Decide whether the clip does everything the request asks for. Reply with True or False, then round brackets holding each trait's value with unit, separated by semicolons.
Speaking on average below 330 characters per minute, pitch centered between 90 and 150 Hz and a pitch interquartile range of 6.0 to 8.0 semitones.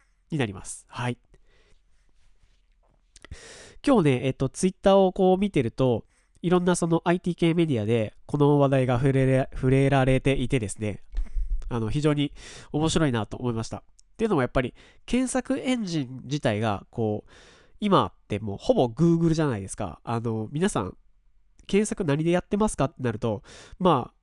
True (320 characters per minute; 135 Hz; 7.1 semitones)